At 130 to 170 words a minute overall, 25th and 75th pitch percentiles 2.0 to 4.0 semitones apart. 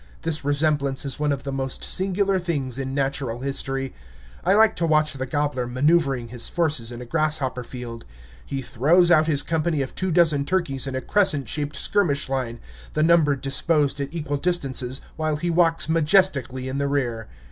No: average, 180 wpm; average, 3.6 semitones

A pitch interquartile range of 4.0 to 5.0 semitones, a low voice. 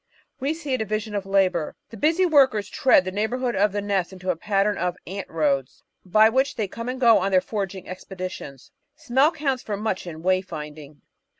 No: average, 4.5 semitones; high, 200 Hz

